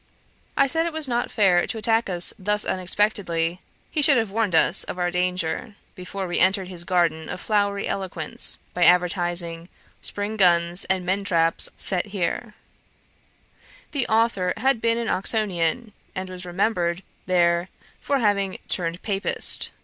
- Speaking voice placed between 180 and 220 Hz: Yes, high, 190 Hz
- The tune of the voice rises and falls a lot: No, average, 3.5 semitones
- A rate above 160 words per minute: No, average, 150 wpm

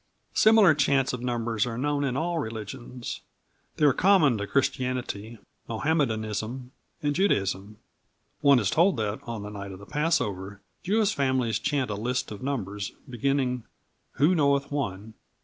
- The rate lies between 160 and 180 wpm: No, average, 150 wpm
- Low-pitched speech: Yes, low, 125 Hz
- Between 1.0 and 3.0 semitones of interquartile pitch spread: No, average, 4.9 semitones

